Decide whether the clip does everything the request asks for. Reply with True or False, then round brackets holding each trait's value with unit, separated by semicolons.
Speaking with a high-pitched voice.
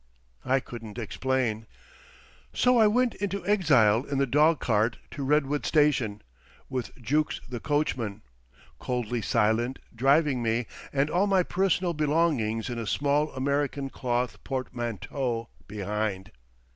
False (130 Hz)